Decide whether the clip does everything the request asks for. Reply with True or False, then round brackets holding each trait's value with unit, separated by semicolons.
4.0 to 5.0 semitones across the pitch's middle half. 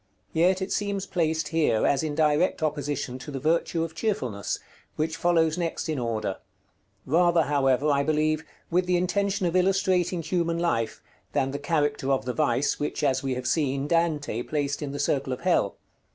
False (3.6 semitones)